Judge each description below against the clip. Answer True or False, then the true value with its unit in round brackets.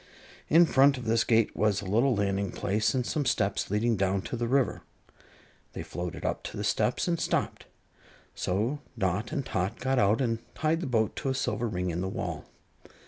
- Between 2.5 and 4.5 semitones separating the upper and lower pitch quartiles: False (5.1 semitones)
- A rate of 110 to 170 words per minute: False (195 wpm)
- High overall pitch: False (115 Hz)